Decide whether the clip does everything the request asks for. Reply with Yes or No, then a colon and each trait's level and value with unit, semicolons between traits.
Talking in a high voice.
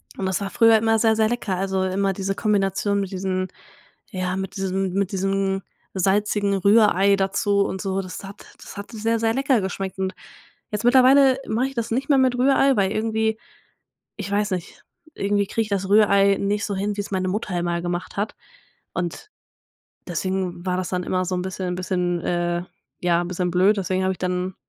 Yes: high, 195 Hz